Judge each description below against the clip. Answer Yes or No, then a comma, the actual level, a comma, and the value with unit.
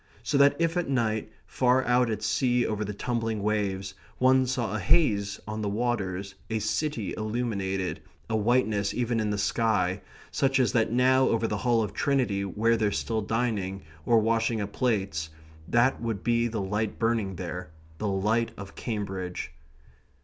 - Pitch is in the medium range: No, low, 110 Hz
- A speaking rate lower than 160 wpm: No, average, 170 wpm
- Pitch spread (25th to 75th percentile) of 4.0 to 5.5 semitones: No, average, 3.1 semitones